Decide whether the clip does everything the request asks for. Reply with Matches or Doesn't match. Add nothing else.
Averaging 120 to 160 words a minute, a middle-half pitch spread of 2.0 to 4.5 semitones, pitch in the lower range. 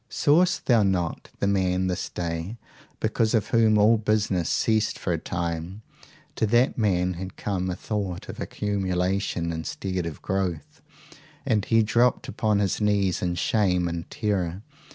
Matches